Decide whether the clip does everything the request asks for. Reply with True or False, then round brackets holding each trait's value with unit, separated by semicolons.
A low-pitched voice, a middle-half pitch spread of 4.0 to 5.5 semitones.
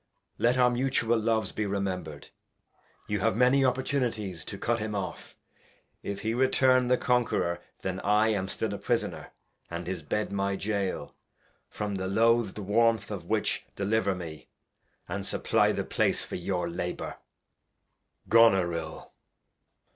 False (105 Hz; 3.6 semitones)